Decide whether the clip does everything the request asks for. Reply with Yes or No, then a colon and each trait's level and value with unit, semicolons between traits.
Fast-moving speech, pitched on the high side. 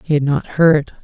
No: fast, 235 wpm; medium, 150 Hz